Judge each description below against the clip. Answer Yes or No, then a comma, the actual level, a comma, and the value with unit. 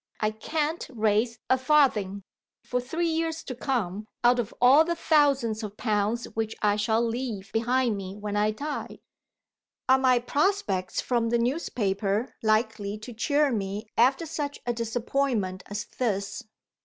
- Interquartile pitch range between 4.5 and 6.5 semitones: No, average, 4.0 semitones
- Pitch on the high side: Yes, high, 235 Hz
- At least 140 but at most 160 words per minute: Yes, average, 150 wpm